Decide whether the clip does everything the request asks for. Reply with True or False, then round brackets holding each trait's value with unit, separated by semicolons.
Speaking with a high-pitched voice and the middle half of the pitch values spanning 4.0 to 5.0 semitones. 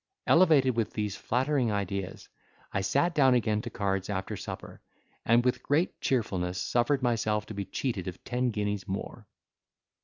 False (110 Hz; 4.6 semitones)